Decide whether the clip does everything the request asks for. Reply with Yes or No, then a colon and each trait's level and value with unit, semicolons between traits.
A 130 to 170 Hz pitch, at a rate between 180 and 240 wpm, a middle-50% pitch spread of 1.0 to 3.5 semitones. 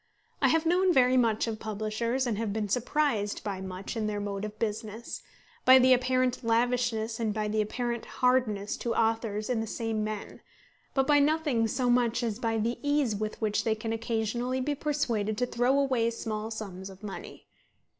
No: high, 230 Hz; average, 185 wpm; average, 2.8 semitones